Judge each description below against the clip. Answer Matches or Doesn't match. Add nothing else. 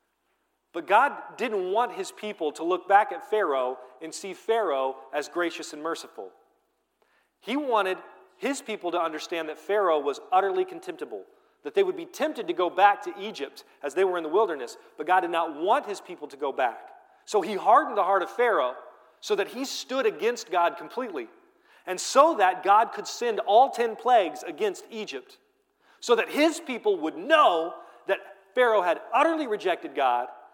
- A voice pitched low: Doesn't match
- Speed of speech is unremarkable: Matches